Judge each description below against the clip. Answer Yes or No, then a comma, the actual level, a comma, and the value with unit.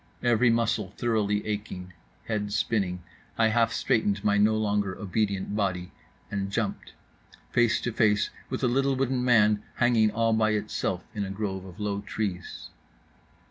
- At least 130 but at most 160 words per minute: Yes, average, 150 wpm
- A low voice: Yes, low, 105 Hz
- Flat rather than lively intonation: Yes, narrow, 2.2 semitones